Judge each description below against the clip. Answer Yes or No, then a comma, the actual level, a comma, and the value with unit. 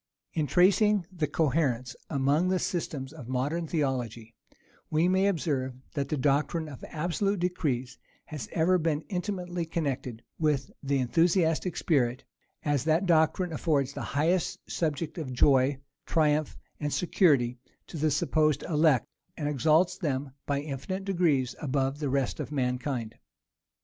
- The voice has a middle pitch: Yes, medium, 150 Hz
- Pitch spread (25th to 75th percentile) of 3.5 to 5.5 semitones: Yes, average, 3.9 semitones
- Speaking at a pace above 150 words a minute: No, average, 140 wpm